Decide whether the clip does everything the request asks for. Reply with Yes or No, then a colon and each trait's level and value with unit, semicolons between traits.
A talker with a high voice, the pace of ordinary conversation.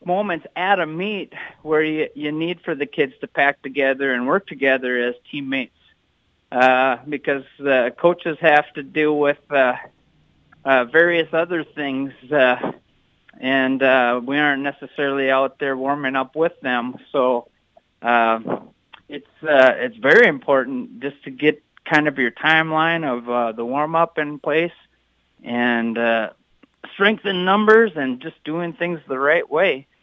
No: medium, 140 Hz; average, 150 wpm